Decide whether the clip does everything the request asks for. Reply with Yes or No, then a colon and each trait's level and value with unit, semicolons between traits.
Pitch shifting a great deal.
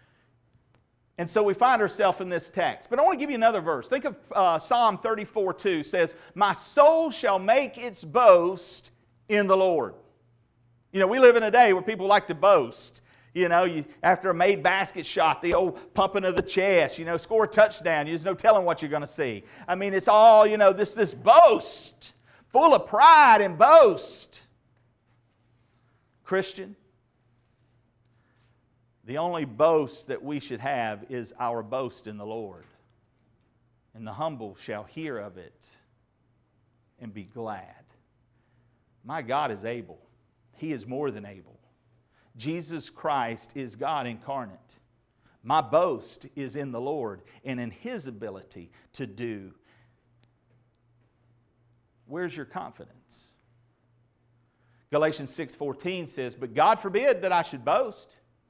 Yes: wide, 7.6 semitones